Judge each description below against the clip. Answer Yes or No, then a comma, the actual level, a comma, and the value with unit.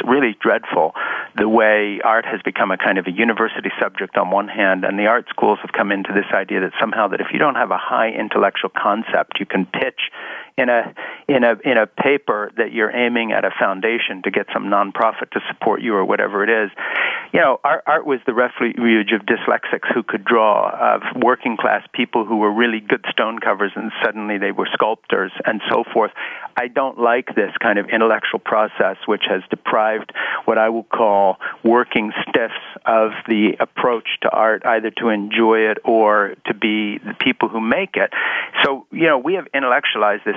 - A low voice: Yes, low, 110 Hz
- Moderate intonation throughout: No, narrow, 1.8 semitones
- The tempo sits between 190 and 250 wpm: Yes, average, 200 wpm